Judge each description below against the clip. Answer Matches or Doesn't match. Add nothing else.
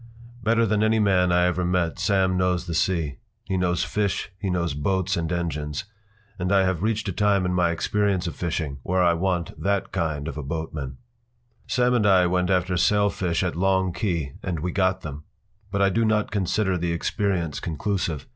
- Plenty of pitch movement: Doesn't match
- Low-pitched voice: Matches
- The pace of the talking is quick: Doesn't match